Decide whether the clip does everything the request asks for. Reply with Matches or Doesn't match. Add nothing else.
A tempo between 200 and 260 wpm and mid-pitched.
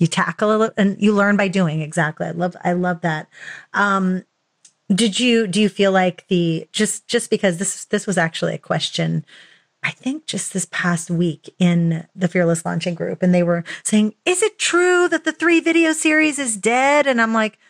Doesn't match